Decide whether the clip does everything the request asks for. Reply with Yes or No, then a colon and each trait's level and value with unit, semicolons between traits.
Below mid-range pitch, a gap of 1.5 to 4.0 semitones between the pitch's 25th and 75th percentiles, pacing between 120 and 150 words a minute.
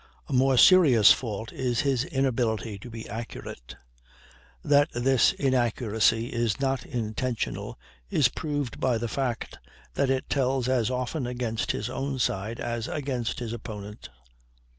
Yes: low, 120 Hz; average, 2.8 semitones; average, 140 wpm